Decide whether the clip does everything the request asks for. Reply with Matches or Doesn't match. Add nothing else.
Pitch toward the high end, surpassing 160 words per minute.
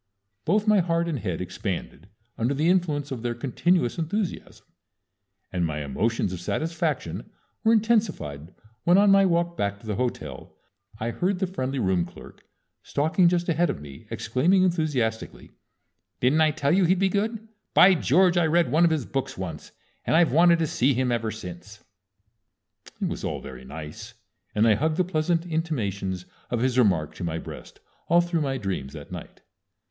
Doesn't match